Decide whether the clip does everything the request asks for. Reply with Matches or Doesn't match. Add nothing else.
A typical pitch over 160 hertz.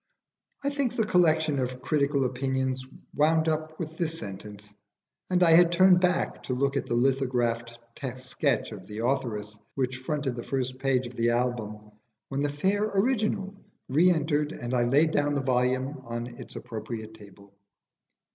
Doesn't match